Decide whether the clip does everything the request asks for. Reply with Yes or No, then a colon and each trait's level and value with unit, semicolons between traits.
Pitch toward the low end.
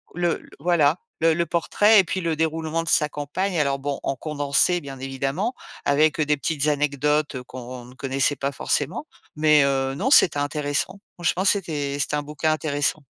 No: medium, 150 Hz